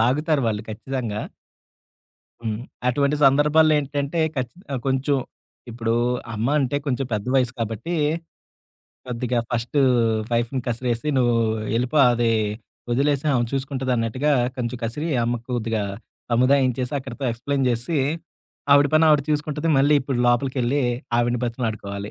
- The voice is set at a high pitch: No, low, 130 Hz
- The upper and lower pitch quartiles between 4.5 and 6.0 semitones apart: No, average, 3.3 semitones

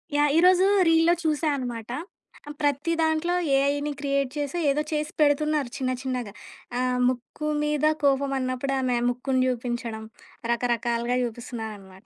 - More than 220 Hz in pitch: Yes, very high, 270 Hz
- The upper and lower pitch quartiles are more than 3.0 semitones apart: Yes, average, 3.6 semitones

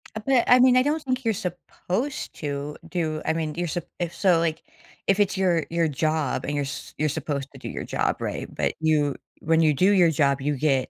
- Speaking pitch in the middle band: Yes, medium, 160 Hz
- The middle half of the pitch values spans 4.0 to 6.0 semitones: Yes, average, 4.4 semitones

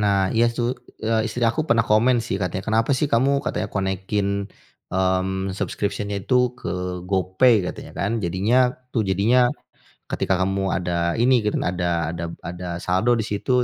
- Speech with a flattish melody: No, average, 3.4 semitones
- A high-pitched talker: No, low, 100 Hz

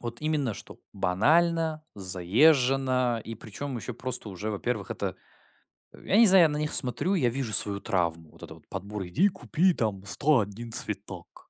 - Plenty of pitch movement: Yes, wide, 6.9 semitones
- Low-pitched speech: Yes, low, 120 Hz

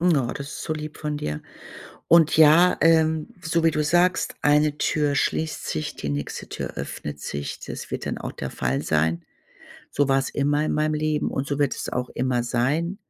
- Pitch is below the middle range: No, medium, 150 Hz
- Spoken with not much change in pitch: No, average, 4.4 semitones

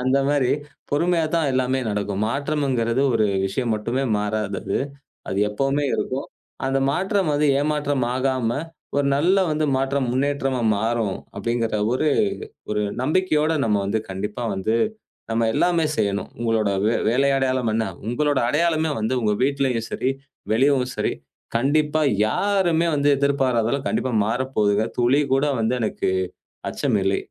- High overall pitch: No, low, 130 Hz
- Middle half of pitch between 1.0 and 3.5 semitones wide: No, average, 4.3 semitones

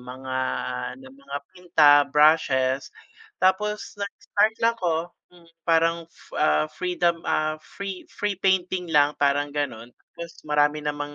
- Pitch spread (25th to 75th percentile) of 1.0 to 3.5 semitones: No, average, 3.9 semitones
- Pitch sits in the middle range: Yes, medium, 160 Hz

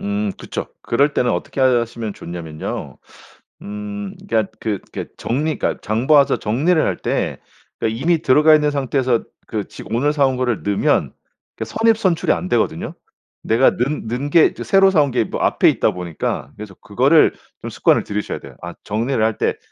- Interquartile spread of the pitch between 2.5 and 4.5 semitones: No, wide, 5.6 semitones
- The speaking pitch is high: No, low, 120 Hz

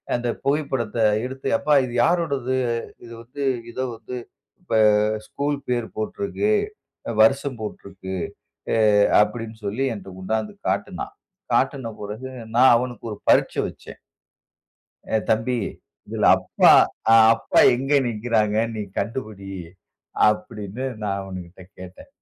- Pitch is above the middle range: No, low, 115 Hz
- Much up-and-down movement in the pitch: No, average, 3.9 semitones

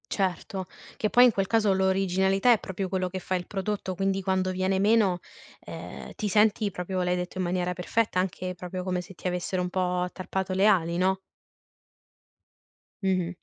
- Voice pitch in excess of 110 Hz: Yes, high, 190 Hz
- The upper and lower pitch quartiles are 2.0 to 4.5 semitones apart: No, narrow, 1.2 semitones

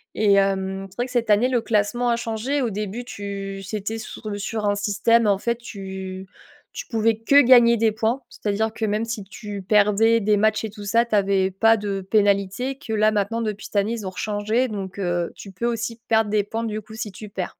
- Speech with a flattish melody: Yes, narrow, 2.3 semitones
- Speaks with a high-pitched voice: Yes, high, 215 Hz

